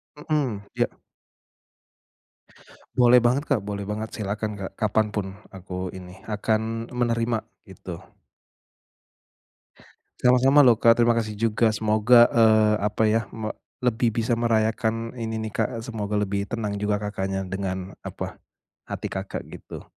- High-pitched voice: No, low, 110 Hz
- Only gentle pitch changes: Yes, narrow, 2.2 semitones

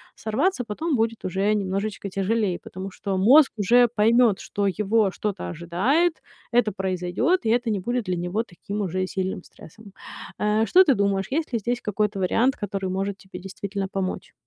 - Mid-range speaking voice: No, high, 205 Hz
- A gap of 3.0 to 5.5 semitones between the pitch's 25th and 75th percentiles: Yes, average, 3.3 semitones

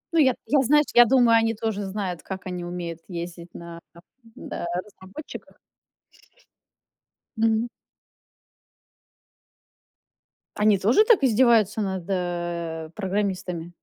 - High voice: Yes, high, 195 Hz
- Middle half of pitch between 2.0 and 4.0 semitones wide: No, average, 4.4 semitones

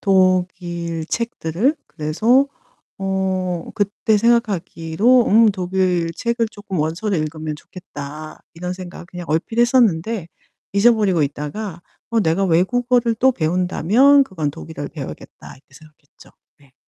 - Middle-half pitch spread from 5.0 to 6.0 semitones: Yes, average, 5.3 semitones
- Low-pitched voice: No, medium, 185 Hz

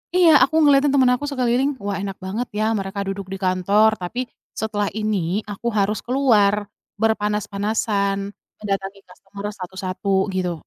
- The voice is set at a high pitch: Yes, high, 205 Hz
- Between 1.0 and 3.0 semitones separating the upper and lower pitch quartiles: Yes, narrow, 2.6 semitones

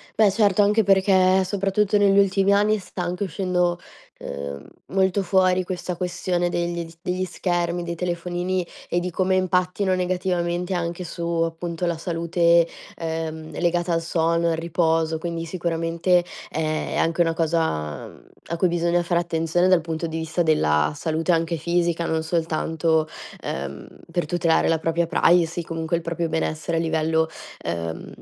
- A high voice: No, medium, 170 Hz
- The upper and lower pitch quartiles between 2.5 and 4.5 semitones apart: No, narrow, 1.8 semitones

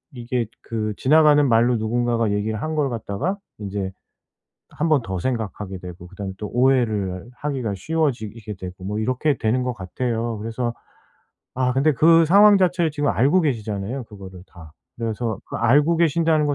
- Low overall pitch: Yes, low, 120 Hz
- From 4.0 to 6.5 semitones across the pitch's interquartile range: Yes, wide, 5.8 semitones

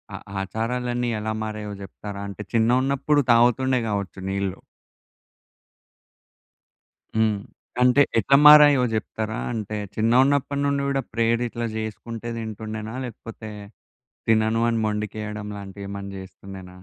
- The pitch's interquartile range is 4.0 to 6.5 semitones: No, average, 2.8 semitones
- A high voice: No, low, 110 Hz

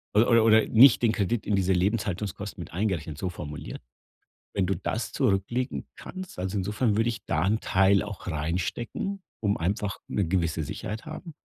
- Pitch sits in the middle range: No, low, 100 Hz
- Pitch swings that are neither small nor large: Yes, average, 3.6 semitones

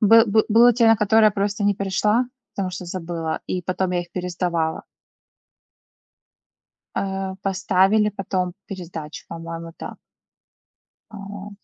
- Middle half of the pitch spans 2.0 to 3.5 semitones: Yes, average, 2.8 semitones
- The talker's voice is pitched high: Yes, high, 195 Hz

